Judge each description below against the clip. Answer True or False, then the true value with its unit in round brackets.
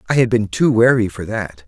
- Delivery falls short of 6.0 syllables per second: True (5.5 syllables/s)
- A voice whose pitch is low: True (105 Hz)